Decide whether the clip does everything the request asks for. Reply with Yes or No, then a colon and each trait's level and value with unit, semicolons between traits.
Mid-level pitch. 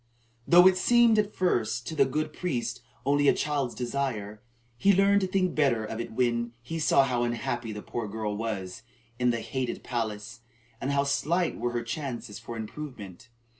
No: low, 125 Hz